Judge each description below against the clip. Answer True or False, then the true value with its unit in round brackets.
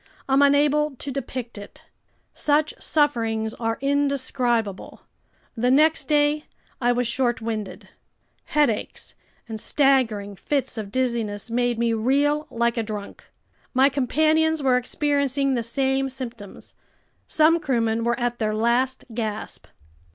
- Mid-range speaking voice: False (250 Hz)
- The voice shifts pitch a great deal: False (3.8 semitones)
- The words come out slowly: True (125 wpm)